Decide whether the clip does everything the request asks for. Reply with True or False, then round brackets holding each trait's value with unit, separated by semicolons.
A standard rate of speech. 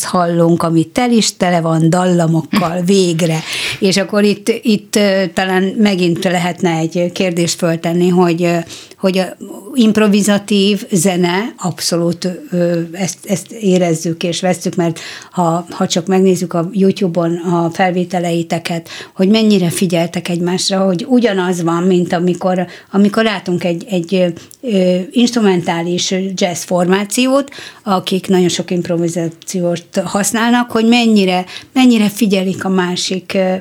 True (115 wpm)